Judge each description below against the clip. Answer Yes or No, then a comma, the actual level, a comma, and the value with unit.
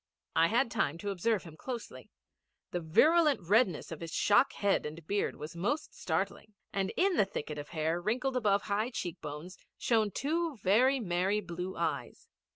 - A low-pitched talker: No, high, 200 Hz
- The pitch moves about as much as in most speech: No, wide, 6.0 semitones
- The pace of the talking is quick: No, average, 170 wpm